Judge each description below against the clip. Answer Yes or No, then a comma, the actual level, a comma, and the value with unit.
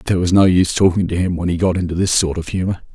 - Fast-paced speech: Yes, fast, 305 wpm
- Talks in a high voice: No, very low, 90 Hz